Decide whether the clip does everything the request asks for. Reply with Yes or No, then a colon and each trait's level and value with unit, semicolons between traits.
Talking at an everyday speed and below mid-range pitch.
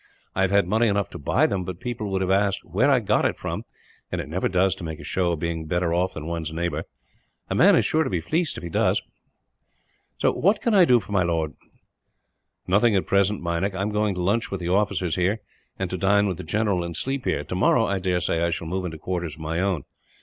No: fast, 245 wpm; very low, 95 Hz